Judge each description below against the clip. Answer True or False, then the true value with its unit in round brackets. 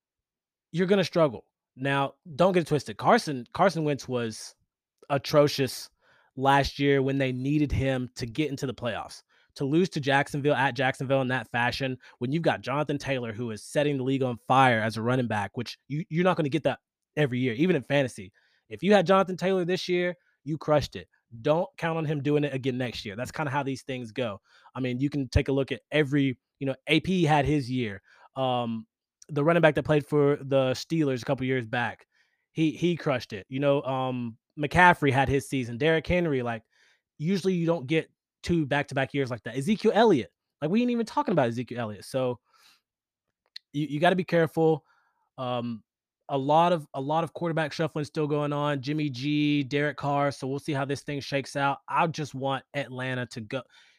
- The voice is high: False (140 Hz)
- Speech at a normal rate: False (210 wpm)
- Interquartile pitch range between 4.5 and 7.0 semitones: False (3.3 semitones)